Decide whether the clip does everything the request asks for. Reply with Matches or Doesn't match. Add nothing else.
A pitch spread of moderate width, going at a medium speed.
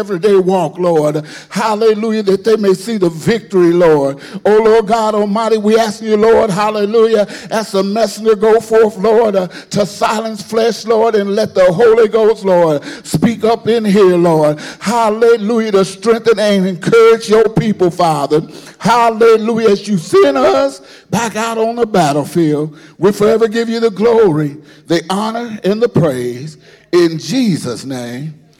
Matches